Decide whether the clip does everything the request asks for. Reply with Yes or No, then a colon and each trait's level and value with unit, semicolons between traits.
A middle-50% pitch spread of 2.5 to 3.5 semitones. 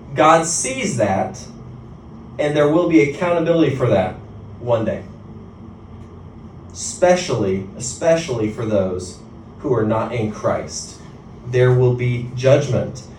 No: average, 4.2 semitones